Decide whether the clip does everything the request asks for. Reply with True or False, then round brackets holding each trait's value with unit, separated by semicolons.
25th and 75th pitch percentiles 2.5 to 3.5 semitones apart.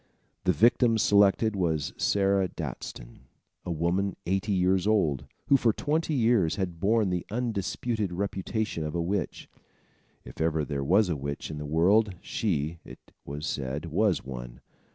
False (5.2 semitones)